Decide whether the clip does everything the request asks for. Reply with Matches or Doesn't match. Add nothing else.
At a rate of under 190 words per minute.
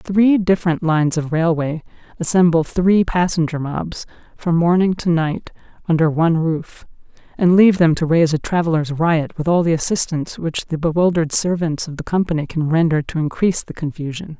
Matches